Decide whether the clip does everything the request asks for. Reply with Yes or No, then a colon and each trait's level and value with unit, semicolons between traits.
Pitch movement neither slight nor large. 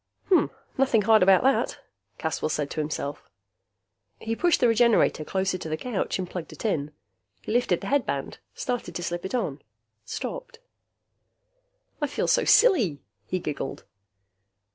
No: wide, 7.6 semitones